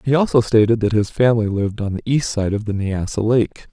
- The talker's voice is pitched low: Yes, low, 110 Hz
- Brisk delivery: Yes, fast, 240 wpm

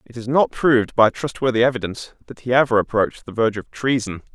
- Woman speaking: No, male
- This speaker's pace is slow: No, fast, 205 wpm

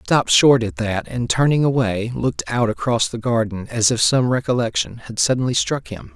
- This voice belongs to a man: Yes, male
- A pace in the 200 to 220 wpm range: Yes, fast, 205 wpm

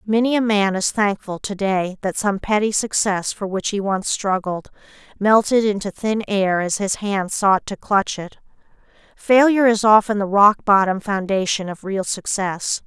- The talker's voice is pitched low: No, high, 200 Hz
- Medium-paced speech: Yes, average, 175 wpm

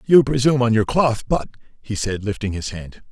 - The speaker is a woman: No, male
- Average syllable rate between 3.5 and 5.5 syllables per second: No, 5.7 syllables/s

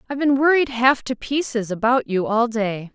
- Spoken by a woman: Yes, female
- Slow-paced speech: No, fast, 205 wpm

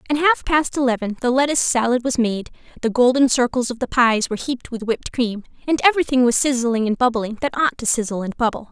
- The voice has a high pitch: Yes, very high, 250 Hz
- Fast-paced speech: Yes, fast, 220 wpm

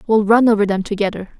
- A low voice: No, high, 210 Hz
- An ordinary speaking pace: No, fast, 215 wpm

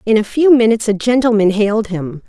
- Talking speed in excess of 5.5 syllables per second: Yes, 6.1 syllables/s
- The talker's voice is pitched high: Yes, high, 220 Hz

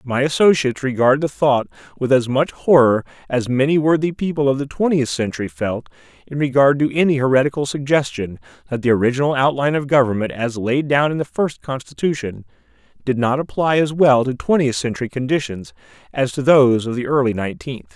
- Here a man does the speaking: Yes, male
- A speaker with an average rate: Yes, average, 175 wpm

